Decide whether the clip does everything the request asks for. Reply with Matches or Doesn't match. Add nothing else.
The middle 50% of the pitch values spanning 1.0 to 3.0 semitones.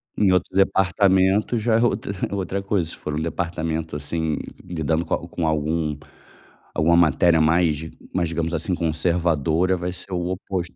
Matches